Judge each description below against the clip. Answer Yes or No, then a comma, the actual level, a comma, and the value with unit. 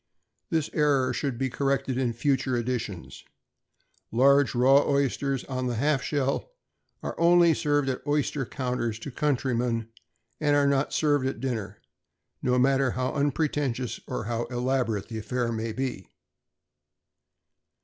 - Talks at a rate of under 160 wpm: Yes, average, 140 wpm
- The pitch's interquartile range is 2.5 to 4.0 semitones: Yes, average, 2.8 semitones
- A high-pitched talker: No, low, 130 Hz